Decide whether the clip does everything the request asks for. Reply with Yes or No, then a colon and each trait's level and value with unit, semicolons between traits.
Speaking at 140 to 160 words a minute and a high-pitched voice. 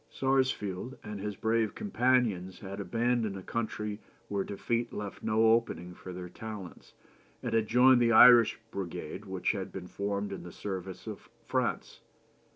No: average, 155 wpm; low, 105 Hz